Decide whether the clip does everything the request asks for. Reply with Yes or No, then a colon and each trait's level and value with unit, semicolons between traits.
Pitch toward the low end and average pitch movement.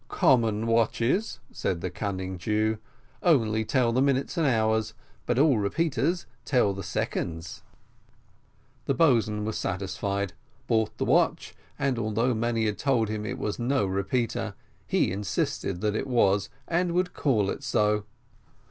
Yes: low, 110 Hz; average, 4.1 semitones